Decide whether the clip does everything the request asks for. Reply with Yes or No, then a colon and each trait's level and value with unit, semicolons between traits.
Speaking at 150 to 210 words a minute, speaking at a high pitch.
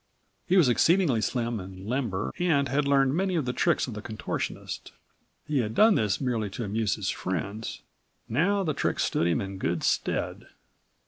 No: average, 180 wpm; low, 120 Hz